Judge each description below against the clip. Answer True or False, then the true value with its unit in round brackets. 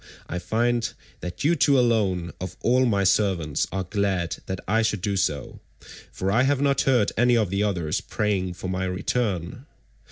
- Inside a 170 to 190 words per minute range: True (180 wpm)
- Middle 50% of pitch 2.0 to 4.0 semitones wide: False (4.5 semitones)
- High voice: False (100 Hz)